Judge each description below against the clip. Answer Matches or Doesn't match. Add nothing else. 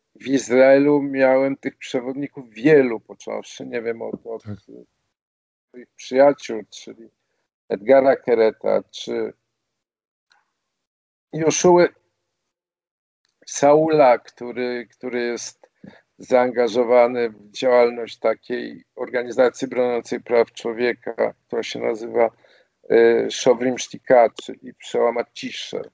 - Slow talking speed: Matches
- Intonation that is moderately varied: Matches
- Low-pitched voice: Matches